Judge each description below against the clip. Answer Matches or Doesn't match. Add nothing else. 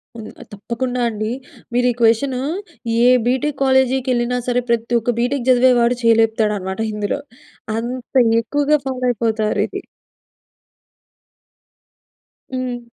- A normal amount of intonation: Doesn't match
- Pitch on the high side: Matches